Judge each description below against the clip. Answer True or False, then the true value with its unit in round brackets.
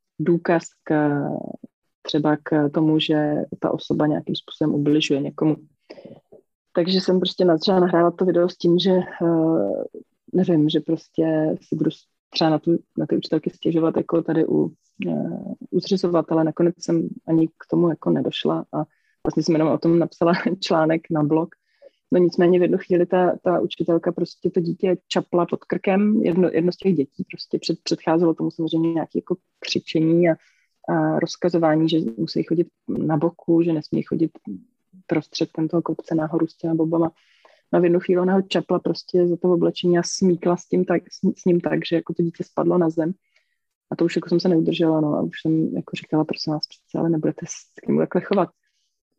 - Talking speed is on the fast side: True (185 wpm)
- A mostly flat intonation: True (1.9 semitones)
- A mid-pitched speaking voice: True (170 Hz)